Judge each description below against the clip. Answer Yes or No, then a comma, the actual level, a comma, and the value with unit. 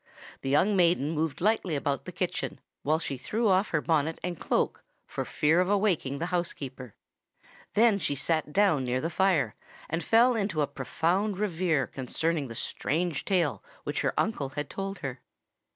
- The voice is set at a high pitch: No, medium, 165 Hz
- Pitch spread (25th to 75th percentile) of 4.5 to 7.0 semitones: Yes, average, 5.1 semitones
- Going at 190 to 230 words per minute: No, average, 170 wpm